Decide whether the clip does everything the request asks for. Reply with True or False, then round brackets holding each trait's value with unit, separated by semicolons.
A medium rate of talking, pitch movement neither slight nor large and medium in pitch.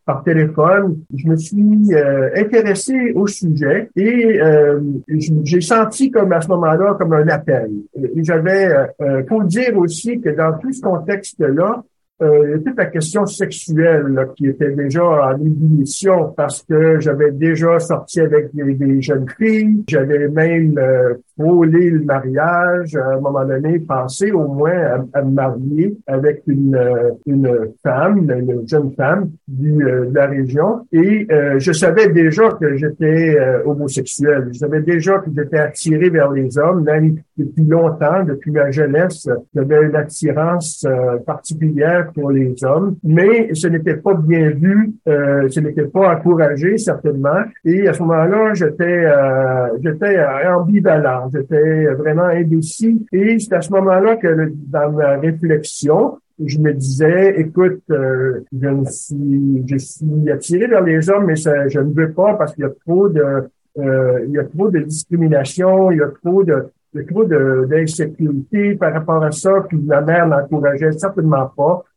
True (165 wpm; 3.9 semitones; 155 Hz)